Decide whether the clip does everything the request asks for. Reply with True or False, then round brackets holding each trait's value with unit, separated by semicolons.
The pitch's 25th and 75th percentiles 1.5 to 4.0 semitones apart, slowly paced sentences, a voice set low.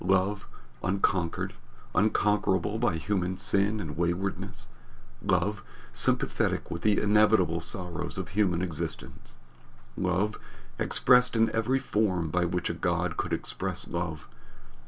True (3.1 semitones; 115 wpm; 95 Hz)